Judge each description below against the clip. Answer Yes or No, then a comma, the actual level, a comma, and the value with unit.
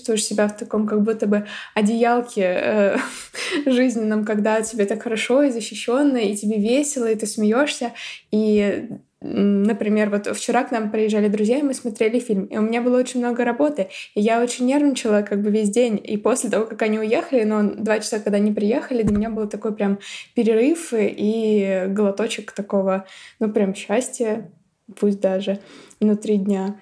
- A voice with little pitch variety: Yes, narrow, 2.3 semitones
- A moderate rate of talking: No, fast, 170 wpm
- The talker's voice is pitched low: No, high, 220 Hz